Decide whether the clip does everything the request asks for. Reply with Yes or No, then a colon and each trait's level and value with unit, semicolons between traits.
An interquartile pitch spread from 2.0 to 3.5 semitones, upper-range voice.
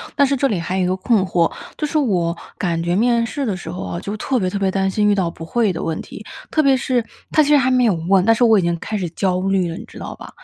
No: average, 5.3 semitones; high, 195 Hz